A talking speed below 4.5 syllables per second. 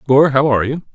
No: 6.7 syllables/s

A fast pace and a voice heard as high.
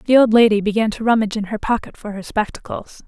Yes: fast, 235 wpm; high, 215 Hz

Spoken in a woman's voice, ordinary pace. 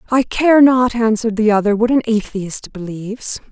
Yes: female; average, 170 wpm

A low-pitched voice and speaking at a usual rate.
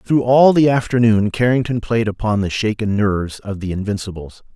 Yes: low, 110 Hz; average, 170 wpm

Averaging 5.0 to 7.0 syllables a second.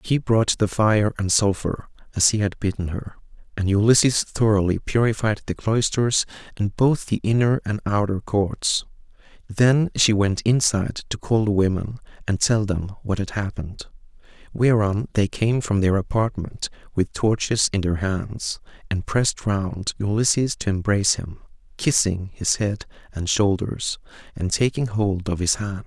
No: 4.5 syllables/s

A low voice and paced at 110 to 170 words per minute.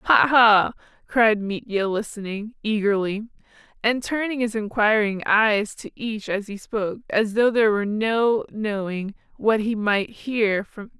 No: high, 215 Hz; average, 155 wpm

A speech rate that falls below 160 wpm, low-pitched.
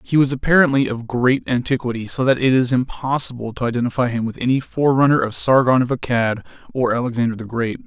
No: average, 190 wpm; low, 125 Hz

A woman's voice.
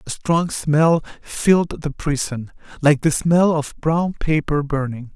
No: male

